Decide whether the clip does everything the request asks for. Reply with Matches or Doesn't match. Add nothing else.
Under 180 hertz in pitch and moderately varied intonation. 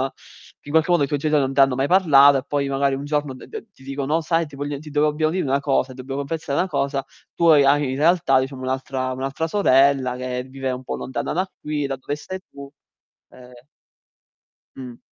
Doesn't match